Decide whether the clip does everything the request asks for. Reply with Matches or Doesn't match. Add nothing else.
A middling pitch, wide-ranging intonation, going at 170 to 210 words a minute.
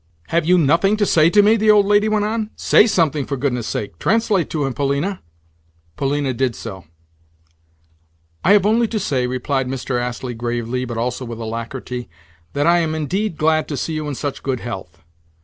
Matches